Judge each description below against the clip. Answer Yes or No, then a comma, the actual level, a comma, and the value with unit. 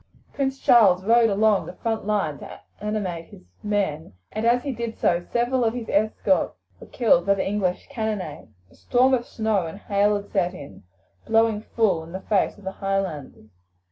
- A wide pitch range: No, average, 3.3 semitones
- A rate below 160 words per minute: No, average, 185 wpm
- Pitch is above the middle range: Yes, high, 210 Hz